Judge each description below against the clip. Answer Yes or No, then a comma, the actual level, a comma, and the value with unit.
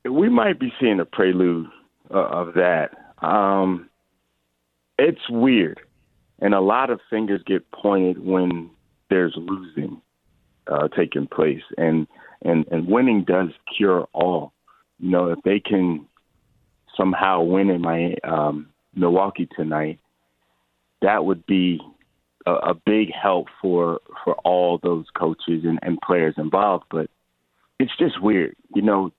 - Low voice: Yes, very low, 85 Hz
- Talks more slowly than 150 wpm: Yes, slow, 135 wpm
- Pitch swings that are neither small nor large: Yes, average, 3.4 semitones